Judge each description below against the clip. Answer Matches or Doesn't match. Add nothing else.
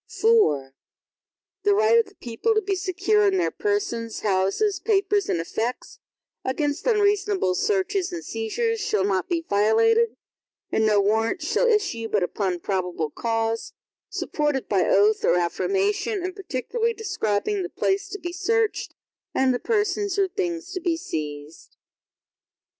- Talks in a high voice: Matches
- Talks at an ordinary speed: Matches